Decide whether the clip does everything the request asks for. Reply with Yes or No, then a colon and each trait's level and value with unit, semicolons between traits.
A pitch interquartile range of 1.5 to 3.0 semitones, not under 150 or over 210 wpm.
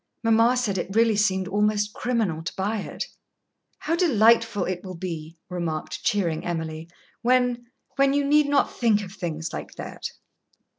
No: average, 5.1 semitones; average, 155 wpm